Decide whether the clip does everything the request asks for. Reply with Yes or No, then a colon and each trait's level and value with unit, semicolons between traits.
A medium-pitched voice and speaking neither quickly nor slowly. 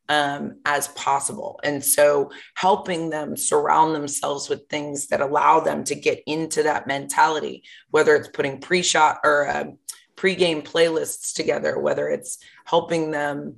Yes: medium, 160 Hz; average, 150 wpm